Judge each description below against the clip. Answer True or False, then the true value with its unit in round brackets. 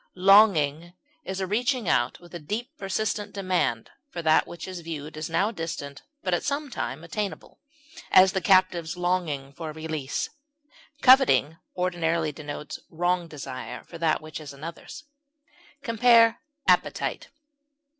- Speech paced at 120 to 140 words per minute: True (135 wpm)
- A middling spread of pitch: True (4.0 semitones)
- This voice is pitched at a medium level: True (175 Hz)